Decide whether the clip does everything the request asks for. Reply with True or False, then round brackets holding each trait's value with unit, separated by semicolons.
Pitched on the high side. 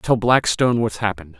False (110 Hz)